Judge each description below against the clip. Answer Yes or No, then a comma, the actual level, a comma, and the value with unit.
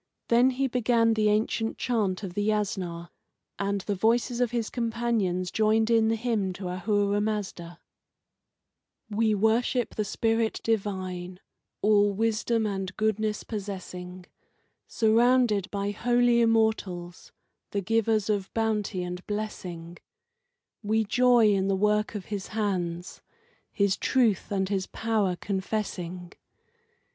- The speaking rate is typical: No, slow, 125 wpm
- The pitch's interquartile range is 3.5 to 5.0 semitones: No, average, 2.9 semitones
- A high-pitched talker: Yes, high, 210 Hz